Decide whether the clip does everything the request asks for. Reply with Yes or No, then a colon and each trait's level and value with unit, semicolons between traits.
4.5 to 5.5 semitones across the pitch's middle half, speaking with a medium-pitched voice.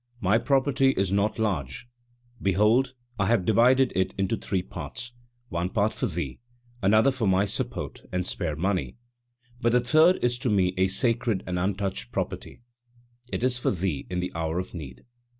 No: average, 4.9 semitones; low, 100 Hz